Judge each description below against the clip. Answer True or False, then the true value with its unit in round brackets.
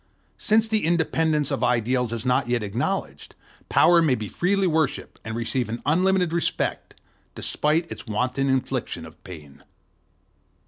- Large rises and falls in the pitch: True (6.0 semitones)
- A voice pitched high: False (135 Hz)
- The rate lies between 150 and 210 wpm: False (140 wpm)